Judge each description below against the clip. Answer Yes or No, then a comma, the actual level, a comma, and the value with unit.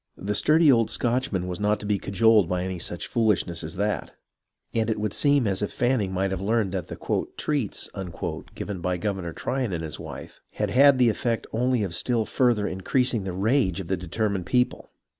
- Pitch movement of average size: Yes, average, 4.4 semitones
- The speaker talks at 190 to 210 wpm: Yes, fast, 205 wpm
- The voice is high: No, low, 105 Hz